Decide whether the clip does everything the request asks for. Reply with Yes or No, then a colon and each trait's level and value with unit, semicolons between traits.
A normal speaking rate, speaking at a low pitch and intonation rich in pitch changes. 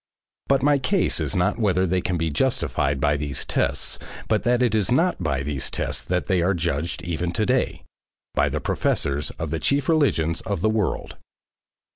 Yes: average, 190 wpm; very low, 90 Hz; wide, 7.1 semitones